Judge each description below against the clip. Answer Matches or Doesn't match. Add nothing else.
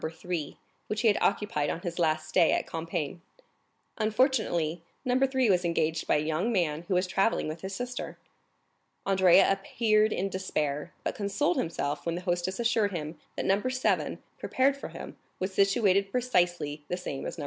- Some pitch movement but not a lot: Matches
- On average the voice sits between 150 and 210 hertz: Matches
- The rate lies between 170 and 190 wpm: Matches